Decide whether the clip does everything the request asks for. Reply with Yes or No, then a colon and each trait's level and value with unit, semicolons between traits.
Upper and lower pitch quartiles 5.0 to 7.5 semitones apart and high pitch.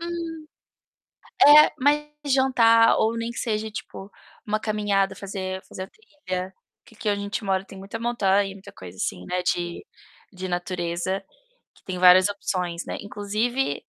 No: average, 3.6 semitones; high, 200 Hz